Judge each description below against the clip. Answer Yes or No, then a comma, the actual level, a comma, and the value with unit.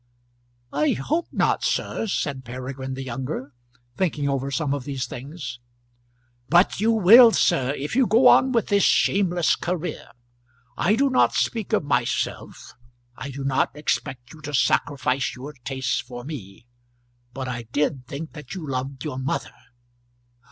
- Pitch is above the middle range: No, medium, 140 Hz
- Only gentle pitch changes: No, average, 5.1 semitones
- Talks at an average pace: Yes, average, 150 wpm